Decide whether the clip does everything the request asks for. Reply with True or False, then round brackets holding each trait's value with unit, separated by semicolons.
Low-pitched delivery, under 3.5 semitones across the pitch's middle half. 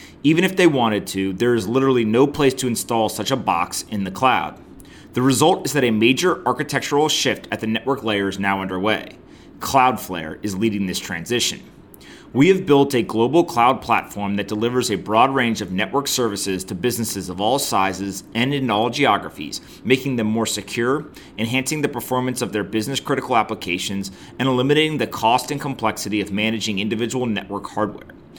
False (115 Hz; 4.4 semitones)